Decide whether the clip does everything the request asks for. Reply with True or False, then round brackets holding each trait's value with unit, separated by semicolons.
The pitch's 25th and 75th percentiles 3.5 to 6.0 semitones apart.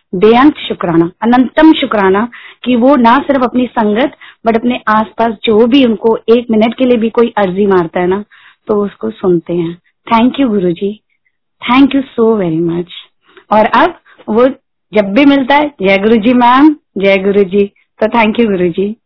True (3.9 semitones)